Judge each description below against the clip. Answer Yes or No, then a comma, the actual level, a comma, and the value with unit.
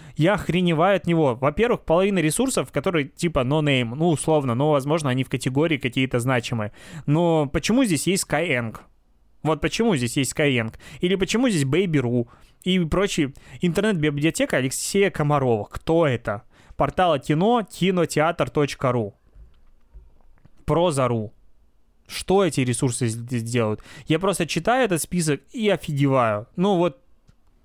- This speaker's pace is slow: No, average, 130 wpm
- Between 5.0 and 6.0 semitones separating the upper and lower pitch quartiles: Yes, wide, 5.6 semitones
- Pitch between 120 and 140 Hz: No, medium, 150 Hz